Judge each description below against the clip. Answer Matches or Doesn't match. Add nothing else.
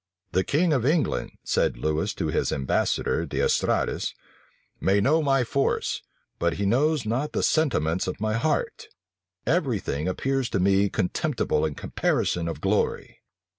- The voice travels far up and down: Matches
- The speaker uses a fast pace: Doesn't match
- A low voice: Matches